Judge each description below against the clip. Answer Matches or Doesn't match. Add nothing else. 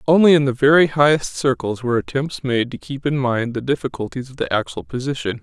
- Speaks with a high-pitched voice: Doesn't match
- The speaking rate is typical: Doesn't match